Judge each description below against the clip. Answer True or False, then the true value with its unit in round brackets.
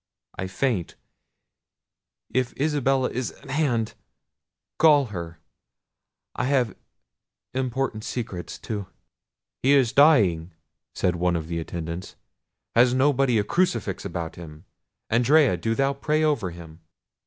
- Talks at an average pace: False (110 wpm)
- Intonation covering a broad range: True (7.6 semitones)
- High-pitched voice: False (115 Hz)